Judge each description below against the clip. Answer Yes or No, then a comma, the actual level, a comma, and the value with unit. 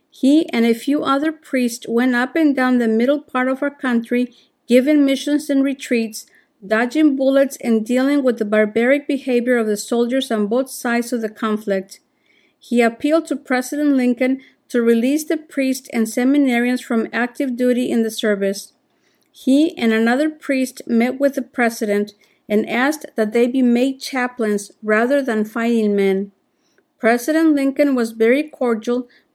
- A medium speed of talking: Yes, average, 160 wpm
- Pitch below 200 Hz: No, very high, 255 Hz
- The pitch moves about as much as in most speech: Yes, average, 3.6 semitones